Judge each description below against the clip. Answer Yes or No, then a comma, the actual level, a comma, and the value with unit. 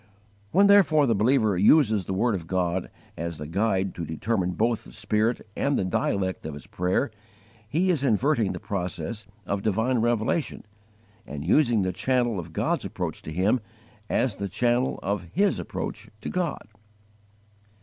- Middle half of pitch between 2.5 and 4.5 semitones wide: No, average, 5.1 semitones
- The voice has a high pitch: No, low, 105 Hz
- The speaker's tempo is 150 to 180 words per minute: Yes, average, 160 wpm